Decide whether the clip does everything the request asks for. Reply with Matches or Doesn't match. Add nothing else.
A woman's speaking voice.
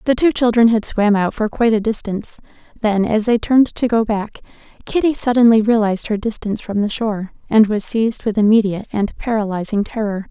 Matches